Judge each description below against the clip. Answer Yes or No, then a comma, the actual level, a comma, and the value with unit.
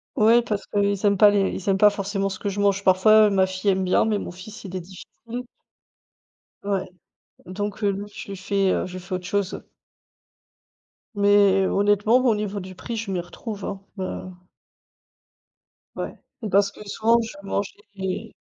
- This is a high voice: Yes, high, 200 Hz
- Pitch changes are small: Yes, narrow, 1.6 semitones